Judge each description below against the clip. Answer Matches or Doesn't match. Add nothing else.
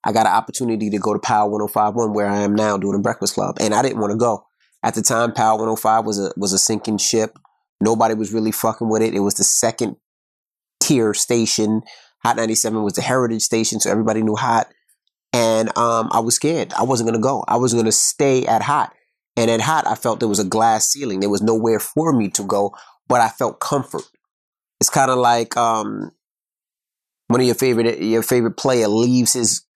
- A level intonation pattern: Matches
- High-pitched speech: Doesn't match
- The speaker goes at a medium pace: Doesn't match